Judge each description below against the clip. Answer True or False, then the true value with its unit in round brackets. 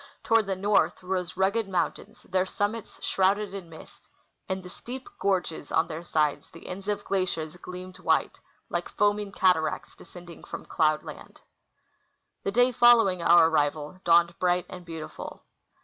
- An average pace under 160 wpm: True (150 wpm)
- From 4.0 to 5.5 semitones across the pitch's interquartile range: False (3.0 semitones)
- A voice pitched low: False (185 Hz)